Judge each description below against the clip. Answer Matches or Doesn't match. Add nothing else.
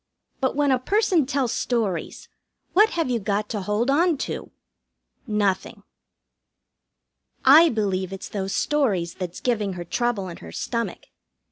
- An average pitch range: Doesn't match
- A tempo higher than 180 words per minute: Doesn't match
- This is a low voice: Doesn't match